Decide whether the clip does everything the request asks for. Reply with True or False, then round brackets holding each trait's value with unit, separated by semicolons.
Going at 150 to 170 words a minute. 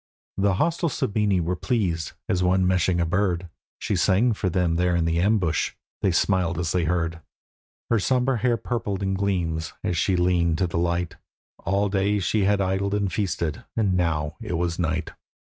False (185 wpm)